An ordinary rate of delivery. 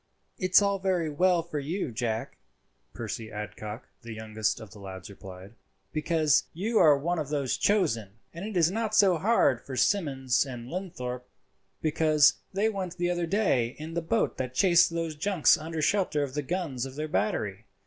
Yes: average, 180 wpm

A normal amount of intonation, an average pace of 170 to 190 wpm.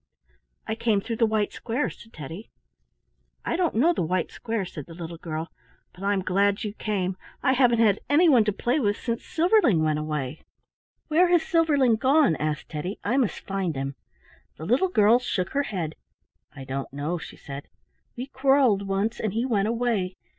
No: wide, 6.4 semitones; average, 180 wpm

